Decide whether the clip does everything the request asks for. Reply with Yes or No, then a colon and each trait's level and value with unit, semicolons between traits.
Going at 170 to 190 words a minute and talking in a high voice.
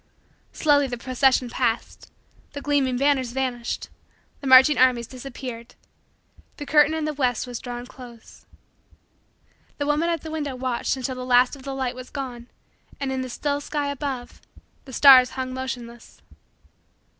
No: average, 155 wpm; very high, 260 Hz